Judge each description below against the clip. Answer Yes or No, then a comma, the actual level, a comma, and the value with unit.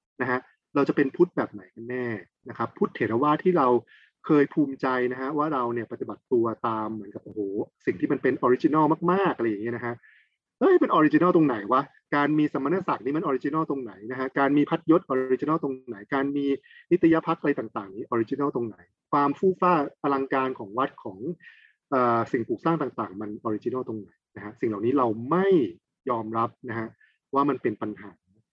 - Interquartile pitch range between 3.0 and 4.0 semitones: No, average, 4.8 semitones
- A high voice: No, low, 135 Hz